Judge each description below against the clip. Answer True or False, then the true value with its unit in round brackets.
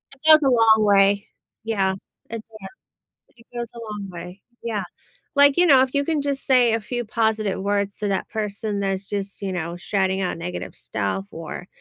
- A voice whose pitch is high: True (205 Hz)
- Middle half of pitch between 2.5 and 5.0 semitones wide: True (3.4 semitones)